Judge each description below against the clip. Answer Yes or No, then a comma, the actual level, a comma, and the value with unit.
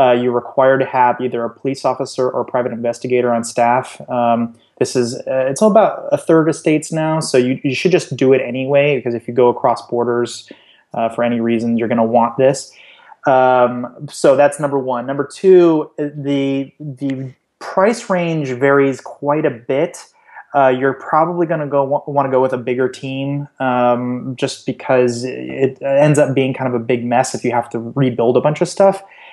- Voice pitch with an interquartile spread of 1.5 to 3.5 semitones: Yes, average, 2.8 semitones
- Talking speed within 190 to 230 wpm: Yes, average, 195 wpm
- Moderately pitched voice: No, low, 130 Hz